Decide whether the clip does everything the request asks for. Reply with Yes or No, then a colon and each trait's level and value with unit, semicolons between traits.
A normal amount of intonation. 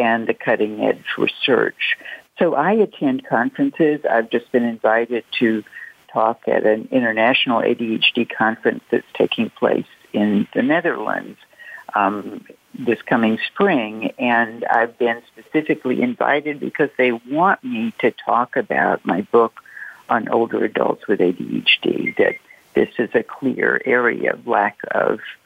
No: wide, 6.4 semitones